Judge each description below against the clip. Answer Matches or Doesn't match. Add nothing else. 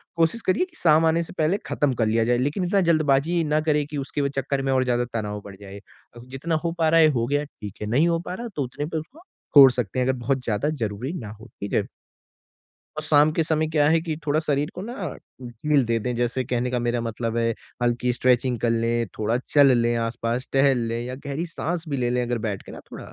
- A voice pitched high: Doesn't match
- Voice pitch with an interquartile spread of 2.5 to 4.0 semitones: Doesn't match